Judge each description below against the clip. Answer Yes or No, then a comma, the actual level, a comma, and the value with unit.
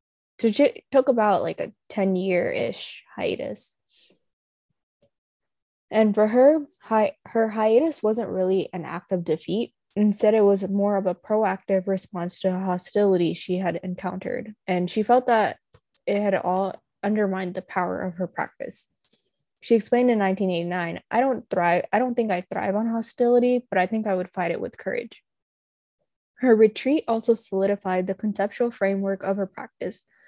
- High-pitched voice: Yes, high, 200 Hz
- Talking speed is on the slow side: No, average, 160 wpm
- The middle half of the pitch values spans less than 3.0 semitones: No, average, 3.5 semitones